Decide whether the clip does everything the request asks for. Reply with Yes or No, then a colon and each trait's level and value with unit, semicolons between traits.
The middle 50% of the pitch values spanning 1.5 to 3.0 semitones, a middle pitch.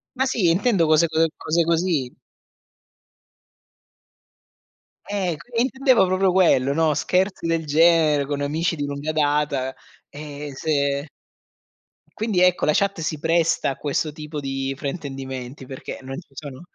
No: average, 3.5 semitones; medium, 155 Hz